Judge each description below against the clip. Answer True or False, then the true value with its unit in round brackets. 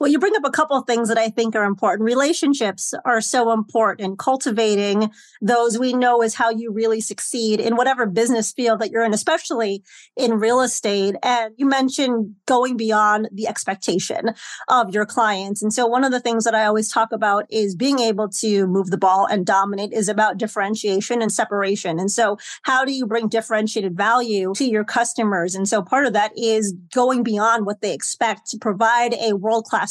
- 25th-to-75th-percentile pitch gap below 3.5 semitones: True (2.4 semitones)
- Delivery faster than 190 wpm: True (200 wpm)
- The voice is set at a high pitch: True (225 Hz)